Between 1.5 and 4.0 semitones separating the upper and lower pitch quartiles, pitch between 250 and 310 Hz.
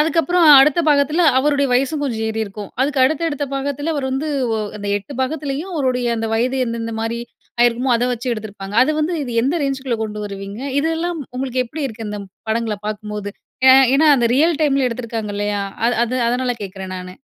No: average, 4.5 semitones; very high, 255 Hz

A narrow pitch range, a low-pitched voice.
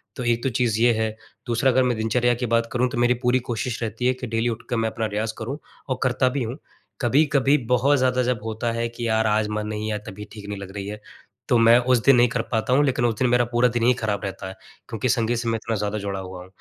Yes: narrow, 2.3 semitones; low, 115 Hz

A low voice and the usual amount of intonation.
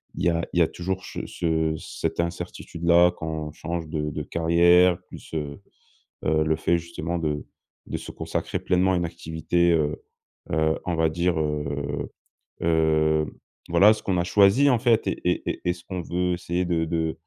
No: very low, 85 Hz; narrow, 2.0 semitones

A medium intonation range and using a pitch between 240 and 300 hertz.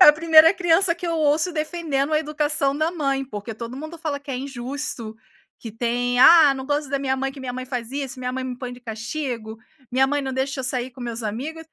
Yes: average, 3.6 semitones; very high, 270 Hz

